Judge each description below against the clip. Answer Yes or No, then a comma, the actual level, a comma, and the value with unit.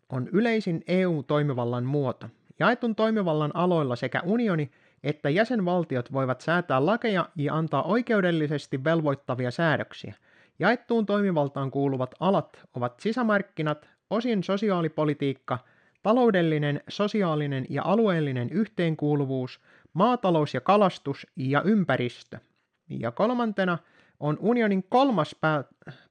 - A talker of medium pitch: Yes, medium, 160 Hz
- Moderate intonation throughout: No, wide, 6.6 semitones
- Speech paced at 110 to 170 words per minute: No, average, 100 wpm